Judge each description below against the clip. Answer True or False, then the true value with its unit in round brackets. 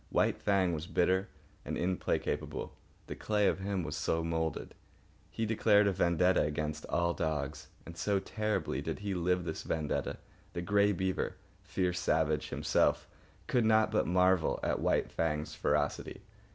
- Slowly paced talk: False (150 wpm)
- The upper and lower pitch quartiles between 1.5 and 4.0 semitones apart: True (3.6 semitones)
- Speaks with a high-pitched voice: False (90 Hz)